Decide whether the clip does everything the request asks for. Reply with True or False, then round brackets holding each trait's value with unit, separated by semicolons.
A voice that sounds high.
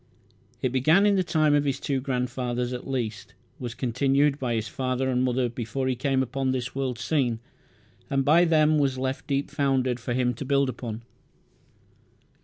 False (130 Hz)